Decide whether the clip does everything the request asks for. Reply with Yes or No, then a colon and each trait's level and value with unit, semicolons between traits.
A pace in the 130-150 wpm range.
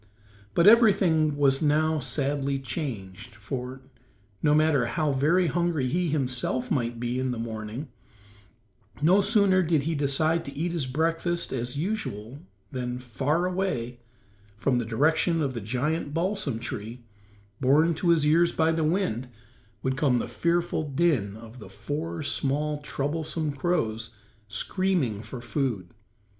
Yes: average, 140 wpm